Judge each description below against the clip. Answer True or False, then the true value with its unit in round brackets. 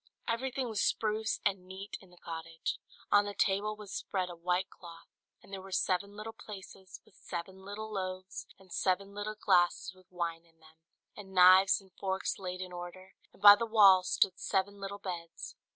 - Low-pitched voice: False (190 Hz)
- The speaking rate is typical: True (185 wpm)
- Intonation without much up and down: True (2.0 semitones)